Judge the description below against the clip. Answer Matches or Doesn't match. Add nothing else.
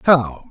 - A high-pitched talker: Doesn't match